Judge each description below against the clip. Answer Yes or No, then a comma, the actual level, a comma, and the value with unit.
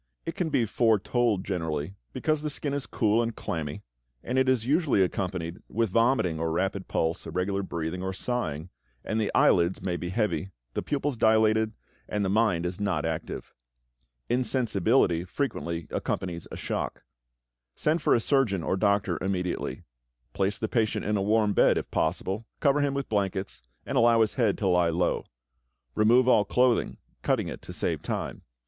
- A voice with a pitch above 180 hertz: No, low, 105 Hz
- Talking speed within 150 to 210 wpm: Yes, average, 170 wpm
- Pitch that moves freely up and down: No, average, 4.8 semitones